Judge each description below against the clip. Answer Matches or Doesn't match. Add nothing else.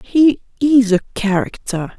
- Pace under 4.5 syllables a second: Matches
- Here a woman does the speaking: Matches